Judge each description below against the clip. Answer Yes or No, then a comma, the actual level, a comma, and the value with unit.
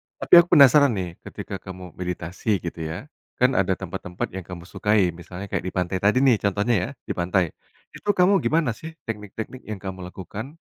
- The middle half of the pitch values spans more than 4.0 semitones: Yes, wide, 5.5 semitones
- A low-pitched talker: Yes, low, 100 Hz